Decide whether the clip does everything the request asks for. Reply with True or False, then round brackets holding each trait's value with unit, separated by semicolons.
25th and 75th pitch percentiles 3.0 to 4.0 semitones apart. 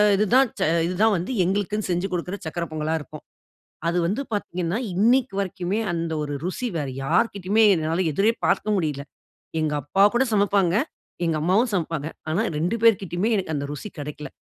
False (4.4 semitones)